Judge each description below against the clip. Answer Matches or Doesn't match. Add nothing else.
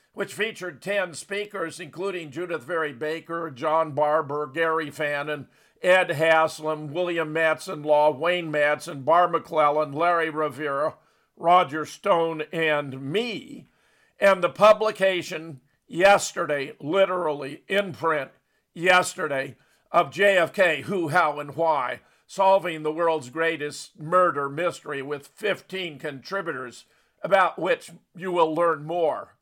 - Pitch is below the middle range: Doesn't match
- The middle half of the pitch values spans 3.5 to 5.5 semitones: Doesn't match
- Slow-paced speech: Matches